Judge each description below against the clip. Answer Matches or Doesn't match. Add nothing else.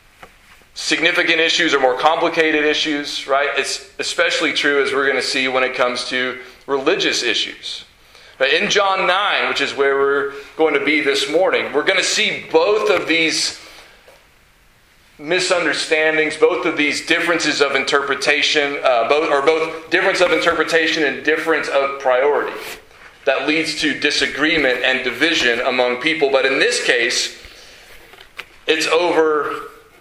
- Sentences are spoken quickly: Doesn't match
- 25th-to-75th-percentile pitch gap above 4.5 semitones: Doesn't match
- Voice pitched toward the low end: Doesn't match